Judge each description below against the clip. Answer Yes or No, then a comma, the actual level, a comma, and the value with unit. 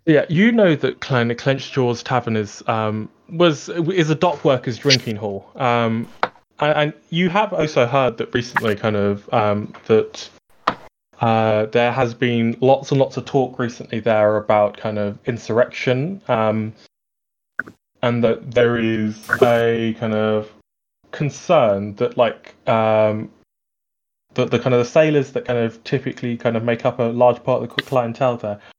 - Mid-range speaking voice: No, low, 120 Hz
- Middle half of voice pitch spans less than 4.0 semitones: Yes, average, 3.3 semitones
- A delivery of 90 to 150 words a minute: No, average, 165 wpm